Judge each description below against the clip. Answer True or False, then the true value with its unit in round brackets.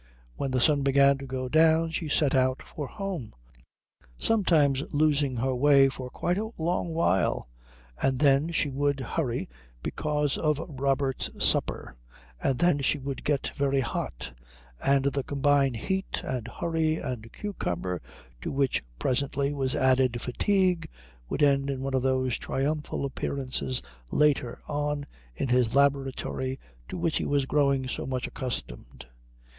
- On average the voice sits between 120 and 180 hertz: True (140 Hz)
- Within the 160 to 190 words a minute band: False (145 wpm)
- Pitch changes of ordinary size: False (2.3 semitones)